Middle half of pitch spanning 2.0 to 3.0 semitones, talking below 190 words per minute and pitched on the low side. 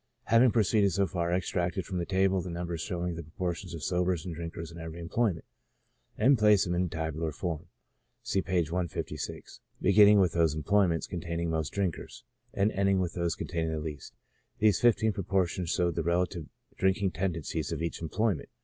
Yes: average, 2.7 semitones; average, 180 wpm; very low, 90 Hz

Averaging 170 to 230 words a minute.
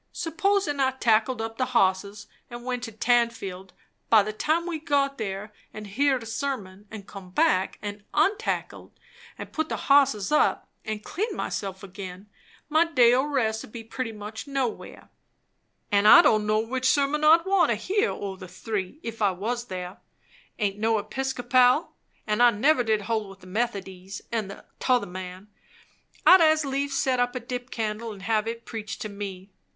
Yes: average, 180 wpm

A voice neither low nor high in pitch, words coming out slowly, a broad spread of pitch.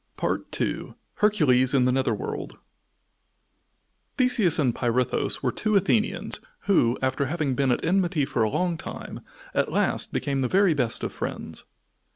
No: medium, 145 Hz; average, 150 wpm; wide, 7.3 semitones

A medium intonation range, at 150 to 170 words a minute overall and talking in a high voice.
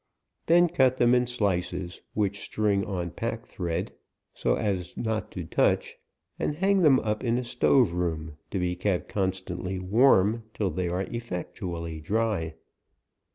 No: average, 4.8 semitones; average, 155 wpm; low, 100 Hz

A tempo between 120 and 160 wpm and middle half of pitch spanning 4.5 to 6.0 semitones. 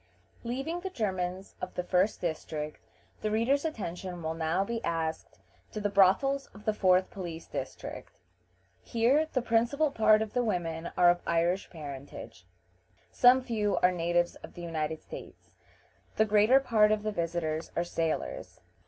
Yes: average, 155 wpm; average, 5.2 semitones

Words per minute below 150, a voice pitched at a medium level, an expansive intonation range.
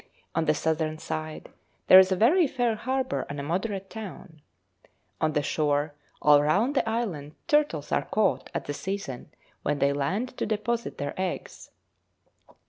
No: average, 160 wpm; medium, 180 Hz; wide, 7.0 semitones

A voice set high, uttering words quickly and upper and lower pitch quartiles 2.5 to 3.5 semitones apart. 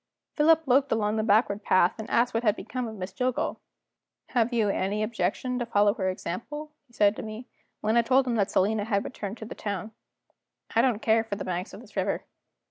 Yes: high, 220 Hz; fast, 215 wpm; average, 3.0 semitones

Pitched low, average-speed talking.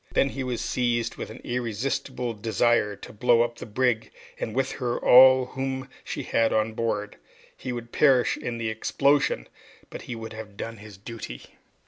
Yes: low, 120 Hz; average, 175 wpm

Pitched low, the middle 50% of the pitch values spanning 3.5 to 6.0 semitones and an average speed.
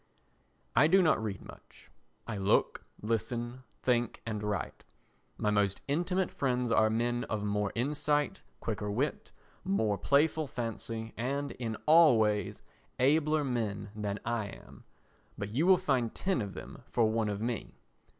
Yes: low, 120 Hz; average, 5.1 semitones; average, 150 wpm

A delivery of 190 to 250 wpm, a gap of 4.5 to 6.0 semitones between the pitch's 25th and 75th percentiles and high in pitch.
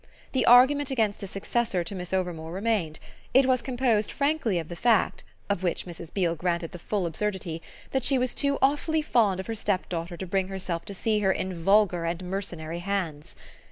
Yes: average, 195 wpm; average, 5.1 semitones; high, 195 Hz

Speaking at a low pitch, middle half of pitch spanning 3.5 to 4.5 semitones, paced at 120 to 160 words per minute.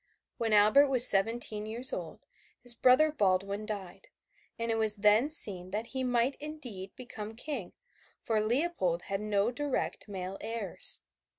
No: high, 220 Hz; average, 3.9 semitones; average, 150 wpm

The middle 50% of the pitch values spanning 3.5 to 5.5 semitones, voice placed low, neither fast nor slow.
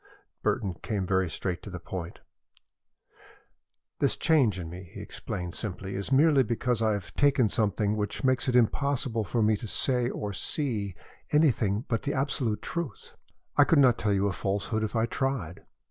Yes: average, 5.0 semitones; low, 110 Hz; average, 175 wpm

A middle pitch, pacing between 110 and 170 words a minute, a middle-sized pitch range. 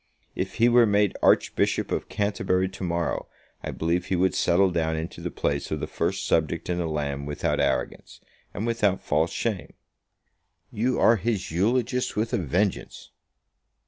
No: very low, 95 Hz; average, 165 wpm; average, 4.4 semitones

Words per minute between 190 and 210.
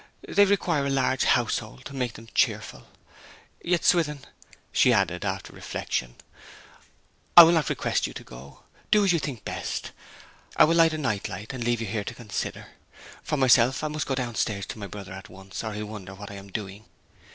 Yes: average, 195 wpm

